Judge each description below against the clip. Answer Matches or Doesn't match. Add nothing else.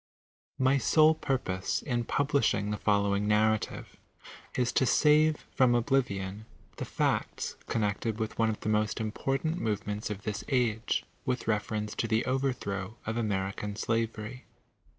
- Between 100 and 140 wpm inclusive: Matches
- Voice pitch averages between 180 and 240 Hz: Doesn't match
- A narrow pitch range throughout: Doesn't match